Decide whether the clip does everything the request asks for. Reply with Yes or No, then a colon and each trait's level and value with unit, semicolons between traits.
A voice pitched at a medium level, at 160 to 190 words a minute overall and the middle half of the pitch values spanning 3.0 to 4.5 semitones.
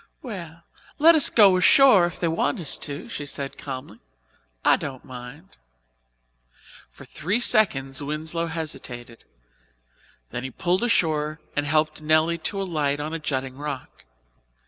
No: medium, 155 Hz; average, 140 wpm; average, 3.6 semitones